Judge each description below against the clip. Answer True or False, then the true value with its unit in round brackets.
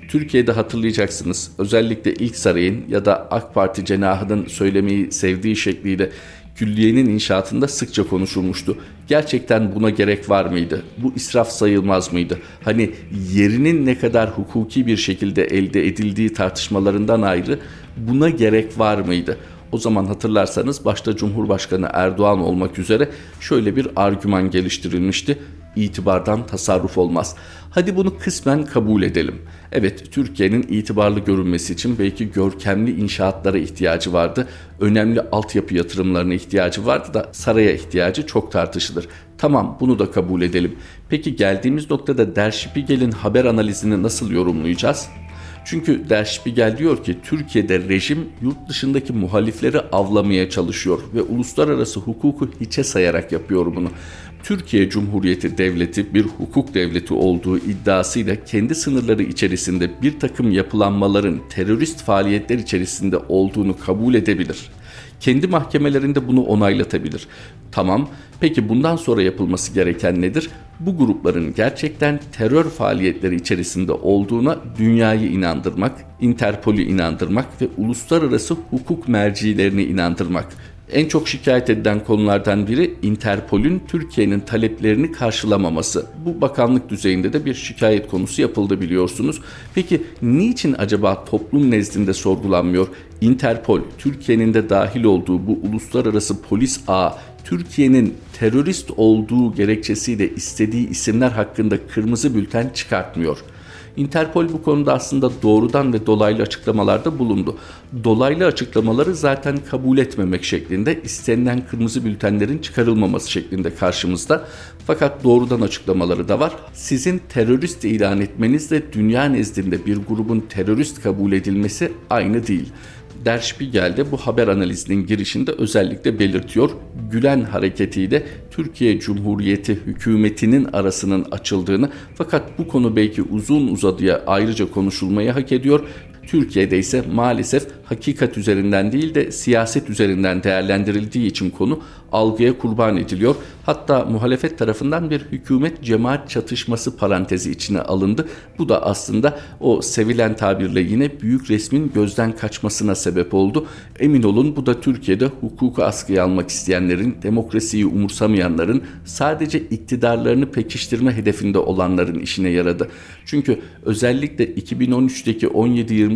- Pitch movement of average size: True (4.6 semitones)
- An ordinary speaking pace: True (120 wpm)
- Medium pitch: False (105 Hz)